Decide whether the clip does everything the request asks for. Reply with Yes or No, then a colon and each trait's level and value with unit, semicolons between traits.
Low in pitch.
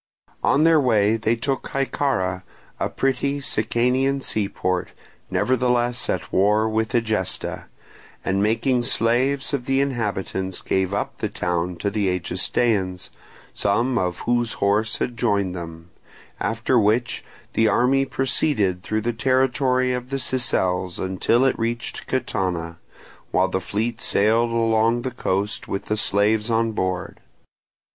Yes: low, 115 Hz